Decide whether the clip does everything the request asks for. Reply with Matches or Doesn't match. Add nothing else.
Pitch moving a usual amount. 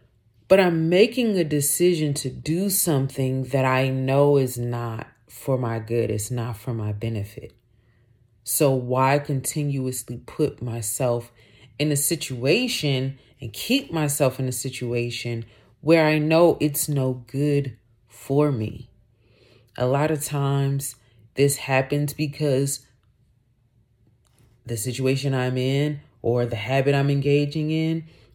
Matches